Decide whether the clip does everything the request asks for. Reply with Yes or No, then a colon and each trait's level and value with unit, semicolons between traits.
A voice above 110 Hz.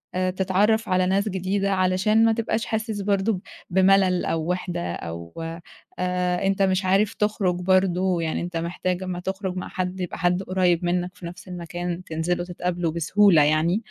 Yes: medium, 185 Hz